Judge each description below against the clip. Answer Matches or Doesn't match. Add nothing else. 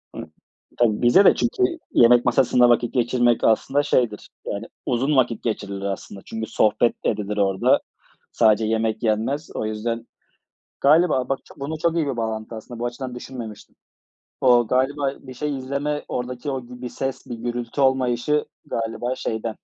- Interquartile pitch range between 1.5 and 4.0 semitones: Matches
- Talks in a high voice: Doesn't match